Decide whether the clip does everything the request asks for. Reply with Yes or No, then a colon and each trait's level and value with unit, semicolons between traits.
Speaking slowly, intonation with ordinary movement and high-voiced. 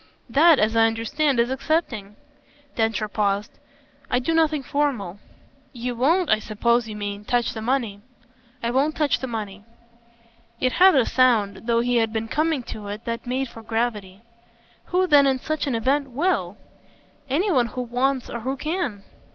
No: average, 170 wpm; average, 4.2 semitones; high, 245 Hz